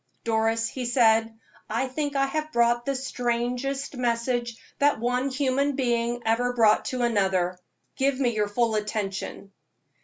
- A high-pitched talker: Yes, high, 240 Hz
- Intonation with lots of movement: No, average, 2.7 semitones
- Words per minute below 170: Yes, average, 145 wpm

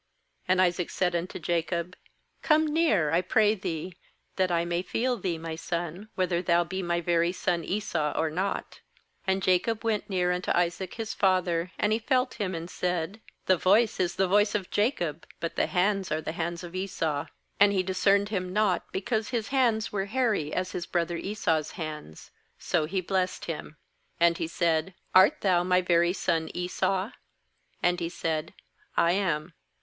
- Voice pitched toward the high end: No, medium, 180 Hz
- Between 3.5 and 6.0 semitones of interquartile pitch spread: No, average, 2.8 semitones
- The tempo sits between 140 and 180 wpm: Yes, average, 175 wpm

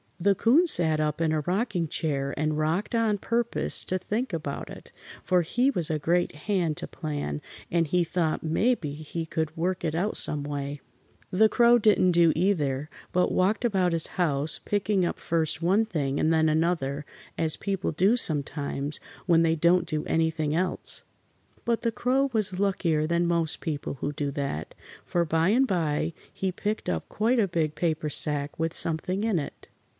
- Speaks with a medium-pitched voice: Yes, medium, 170 Hz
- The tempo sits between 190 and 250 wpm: No, average, 180 wpm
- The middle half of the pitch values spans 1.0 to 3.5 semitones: No, average, 4.2 semitones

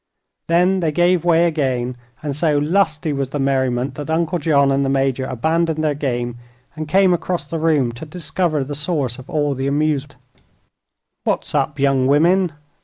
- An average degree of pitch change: Yes, average, 3.4 semitones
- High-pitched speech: No, medium, 150 Hz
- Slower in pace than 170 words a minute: No, average, 175 wpm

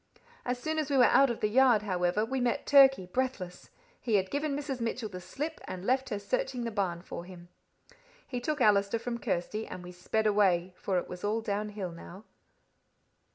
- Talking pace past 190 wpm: Yes, average, 200 wpm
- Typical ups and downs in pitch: No, wide, 5.7 semitones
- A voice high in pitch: Yes, high, 215 Hz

